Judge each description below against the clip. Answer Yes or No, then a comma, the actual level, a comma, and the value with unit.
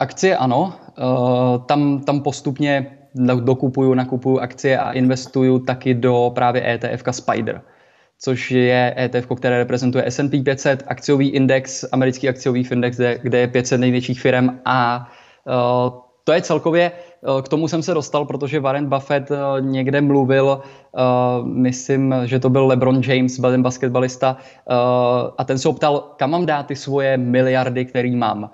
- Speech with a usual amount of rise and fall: No, narrow, 1.7 semitones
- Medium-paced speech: Yes, average, 140 wpm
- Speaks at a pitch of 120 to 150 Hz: Yes, low, 130 Hz